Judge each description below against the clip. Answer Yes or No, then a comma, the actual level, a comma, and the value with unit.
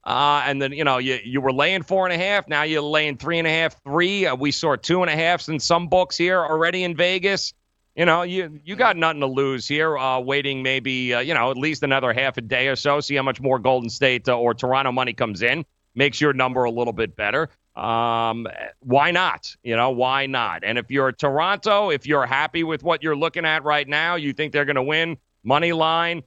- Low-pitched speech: No, medium, 145 Hz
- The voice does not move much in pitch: No, average, 4.1 semitones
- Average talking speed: No, fast, 245 wpm